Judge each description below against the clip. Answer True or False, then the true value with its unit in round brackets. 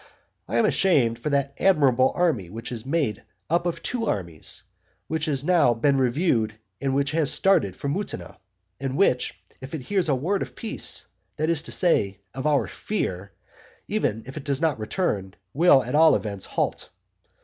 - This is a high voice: False (140 Hz)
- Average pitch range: False (6.0 semitones)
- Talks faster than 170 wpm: True (180 wpm)